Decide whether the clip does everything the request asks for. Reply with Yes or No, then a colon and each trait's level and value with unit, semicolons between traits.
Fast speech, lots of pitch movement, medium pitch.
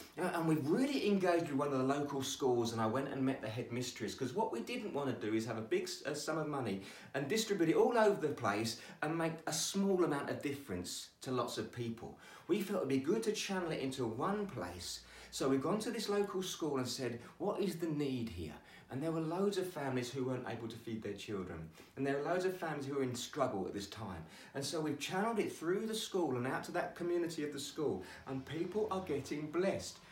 Yes: fast, 245 wpm; wide, 6.5 semitones; medium, 145 Hz